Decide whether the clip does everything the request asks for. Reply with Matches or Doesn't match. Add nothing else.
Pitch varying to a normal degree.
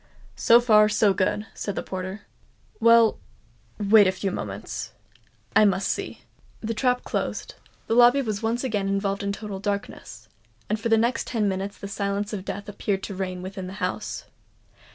Doesn't match